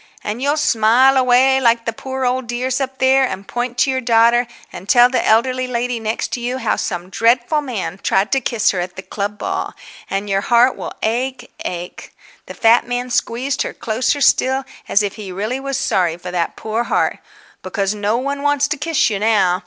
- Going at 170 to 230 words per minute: Yes, average, 200 wpm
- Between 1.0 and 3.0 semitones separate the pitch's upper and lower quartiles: No, average, 3.8 semitones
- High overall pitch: Yes, high, 240 Hz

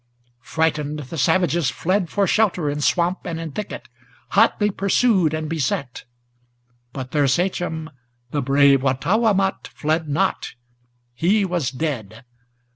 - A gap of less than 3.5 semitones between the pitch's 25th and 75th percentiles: No, average, 4.8 semitones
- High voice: No, medium, 160 Hz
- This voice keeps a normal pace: No, slow, 120 wpm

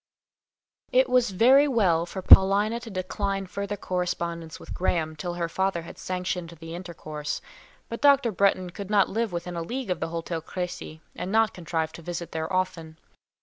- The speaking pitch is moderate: Yes, medium, 180 Hz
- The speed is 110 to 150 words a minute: No, average, 175 wpm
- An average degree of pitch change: Yes, average, 3.2 semitones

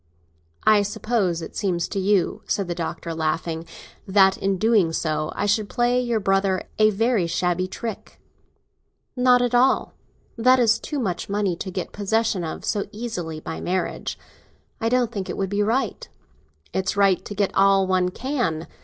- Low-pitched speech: No, high, 195 Hz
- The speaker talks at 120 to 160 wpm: No, average, 170 wpm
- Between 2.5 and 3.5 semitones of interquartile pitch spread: No, average, 3.9 semitones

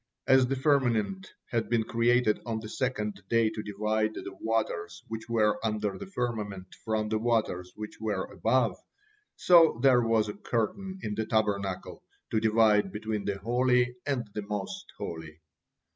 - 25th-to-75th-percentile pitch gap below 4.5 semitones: Yes, narrow, 2.4 semitones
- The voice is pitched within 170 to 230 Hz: No, low, 110 Hz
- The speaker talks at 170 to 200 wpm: No, average, 160 wpm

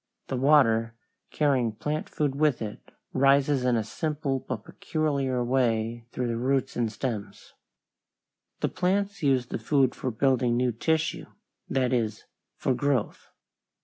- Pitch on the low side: Yes, low, 130 Hz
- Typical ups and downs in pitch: Yes, average, 3.3 semitones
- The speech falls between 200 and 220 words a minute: No, average, 140 wpm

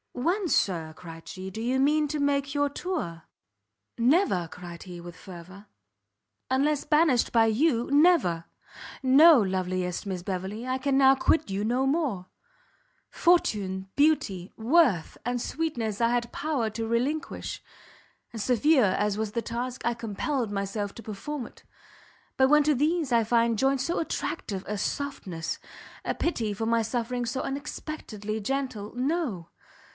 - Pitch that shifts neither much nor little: No, wide, 6.1 semitones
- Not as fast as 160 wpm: Yes, average, 150 wpm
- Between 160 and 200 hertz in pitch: No, high, 235 Hz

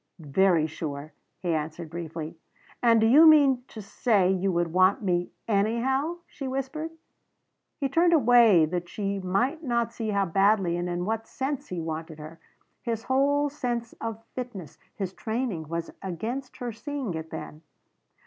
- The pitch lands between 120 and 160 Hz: No, high, 205 Hz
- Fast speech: No, average, 160 wpm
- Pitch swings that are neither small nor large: No, wide, 6.4 semitones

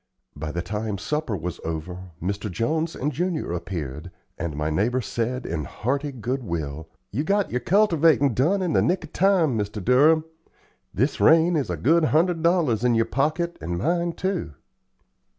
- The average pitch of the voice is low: Yes, low, 125 Hz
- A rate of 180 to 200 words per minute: No, average, 170 wpm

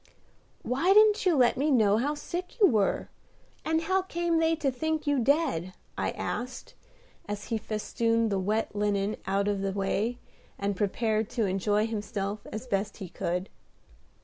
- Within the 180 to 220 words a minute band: No, average, 165 wpm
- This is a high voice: Yes, high, 225 Hz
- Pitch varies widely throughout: Yes, wide, 6.8 semitones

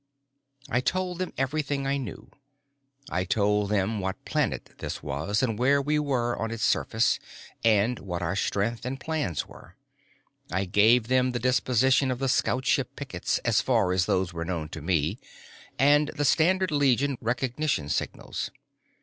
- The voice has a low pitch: Yes, low, 120 Hz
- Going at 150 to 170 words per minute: Yes, average, 160 wpm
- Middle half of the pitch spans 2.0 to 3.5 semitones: No, wide, 5.6 semitones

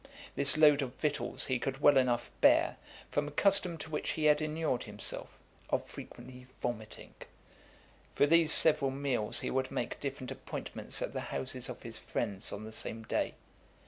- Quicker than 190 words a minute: No, average, 175 wpm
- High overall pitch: No, low, 135 Hz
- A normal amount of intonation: Yes, average, 3.6 semitones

